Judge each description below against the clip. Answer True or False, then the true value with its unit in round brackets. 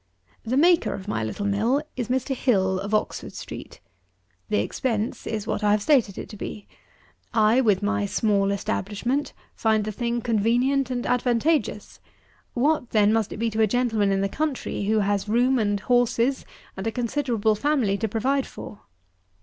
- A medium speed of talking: True (175 wpm)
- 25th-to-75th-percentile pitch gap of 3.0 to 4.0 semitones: True (3.4 semitones)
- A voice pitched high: True (225 Hz)